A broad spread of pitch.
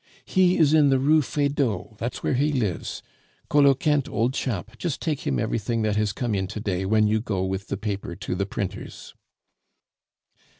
Yes: wide, 6.1 semitones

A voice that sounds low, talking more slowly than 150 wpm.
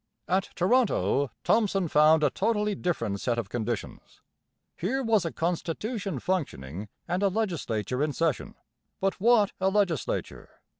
No: medium, 180 Hz; slow, 135 wpm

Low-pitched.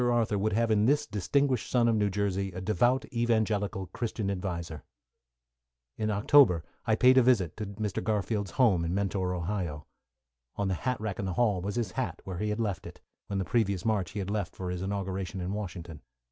Yes: low, 100 Hz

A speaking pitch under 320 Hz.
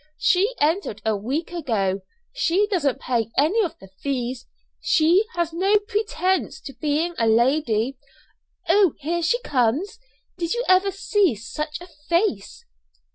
No: very high, 325 Hz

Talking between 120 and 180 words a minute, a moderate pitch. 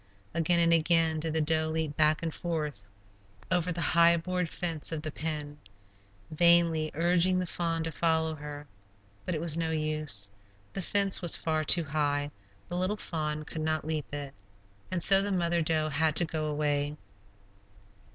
Yes: average, 170 wpm; medium, 160 Hz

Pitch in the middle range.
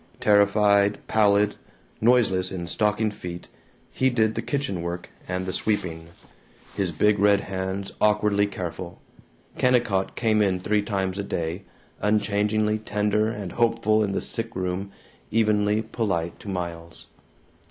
No: low, 100 Hz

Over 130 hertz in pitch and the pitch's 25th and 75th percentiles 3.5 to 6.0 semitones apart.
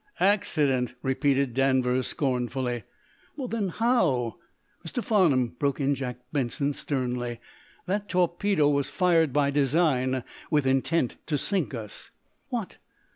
Yes: medium, 140 Hz; average, 5.1 semitones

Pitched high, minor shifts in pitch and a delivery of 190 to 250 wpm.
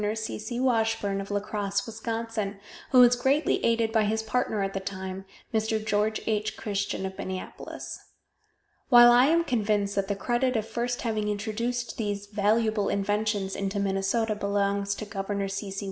No: high, 210 Hz; narrow, 2.2 semitones; average, 165 wpm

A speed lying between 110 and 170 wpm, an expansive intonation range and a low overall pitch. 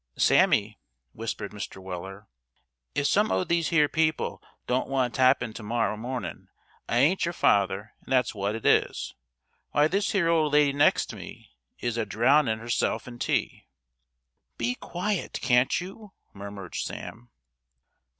Yes: average, 150 wpm; wide, 6.0 semitones; low, 125 Hz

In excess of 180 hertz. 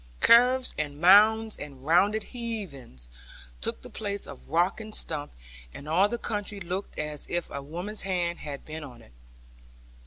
No: medium, 175 Hz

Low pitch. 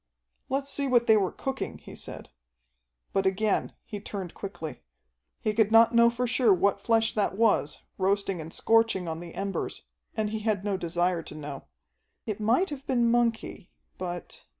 No: high, 210 Hz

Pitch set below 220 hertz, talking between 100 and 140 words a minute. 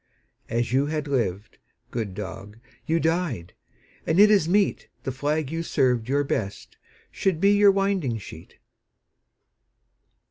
Yes: medium, 140 Hz; slow, 135 wpm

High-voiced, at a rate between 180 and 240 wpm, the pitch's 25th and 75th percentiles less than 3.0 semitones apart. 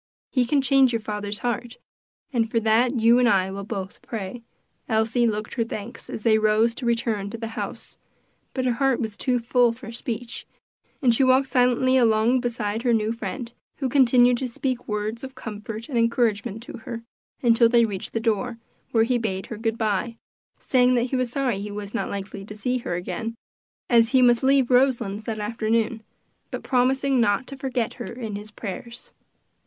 Yes: high, 230 Hz; average, 190 wpm; narrow, 2.4 semitones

